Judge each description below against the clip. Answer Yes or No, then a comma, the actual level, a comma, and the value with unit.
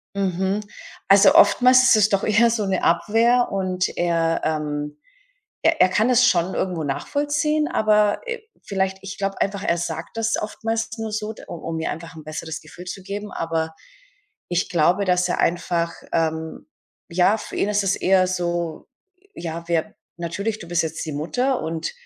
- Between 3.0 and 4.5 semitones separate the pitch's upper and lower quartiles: Yes, average, 4.2 semitones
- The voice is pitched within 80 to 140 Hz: No, medium, 185 Hz